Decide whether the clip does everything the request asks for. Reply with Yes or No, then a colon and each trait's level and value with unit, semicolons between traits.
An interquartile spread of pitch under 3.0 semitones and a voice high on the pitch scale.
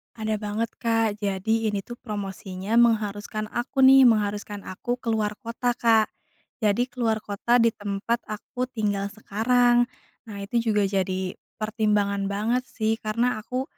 Yes: narrow, 2.4 semitones; high, 215 Hz